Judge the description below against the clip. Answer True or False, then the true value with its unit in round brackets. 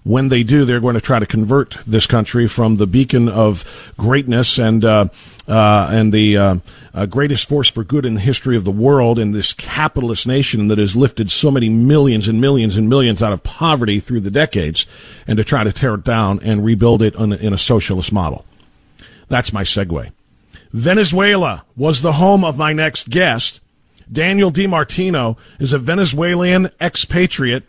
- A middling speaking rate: True (185 wpm)